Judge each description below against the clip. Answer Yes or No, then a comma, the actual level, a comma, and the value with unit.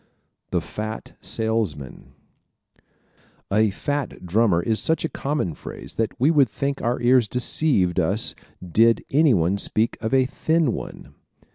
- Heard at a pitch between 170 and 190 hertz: No, low, 115 Hz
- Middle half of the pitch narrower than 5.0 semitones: No, average, 5.3 semitones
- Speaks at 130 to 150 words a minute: Yes, average, 140 wpm